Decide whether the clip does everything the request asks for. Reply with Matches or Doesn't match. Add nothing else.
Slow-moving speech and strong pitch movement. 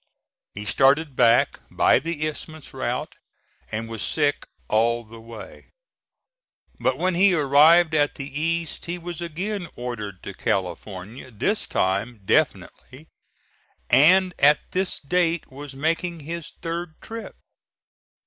Matches